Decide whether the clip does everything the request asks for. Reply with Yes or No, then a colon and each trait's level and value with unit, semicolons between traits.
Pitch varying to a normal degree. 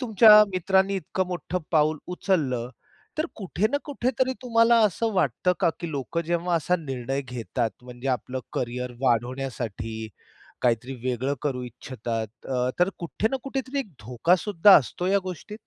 No: wide, 7.6 semitones